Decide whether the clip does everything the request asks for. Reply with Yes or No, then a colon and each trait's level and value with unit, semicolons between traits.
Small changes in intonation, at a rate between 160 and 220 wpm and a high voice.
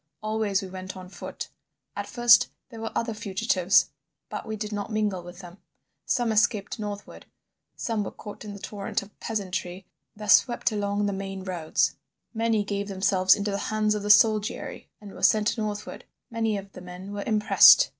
Yes: narrow, 1.9 semitones; average, 180 wpm; high, 205 Hz